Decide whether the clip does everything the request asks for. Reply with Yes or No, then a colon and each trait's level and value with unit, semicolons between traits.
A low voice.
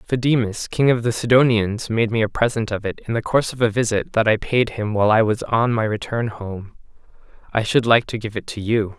Yes: low, 110 Hz